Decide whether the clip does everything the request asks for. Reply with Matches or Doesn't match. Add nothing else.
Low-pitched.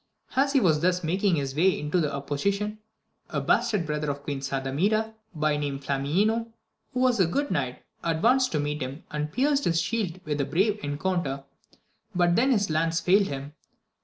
Doesn't match